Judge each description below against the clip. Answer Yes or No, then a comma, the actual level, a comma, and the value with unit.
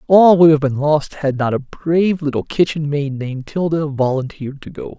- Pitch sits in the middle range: Yes, medium, 150 Hz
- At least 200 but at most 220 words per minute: Yes, fast, 205 wpm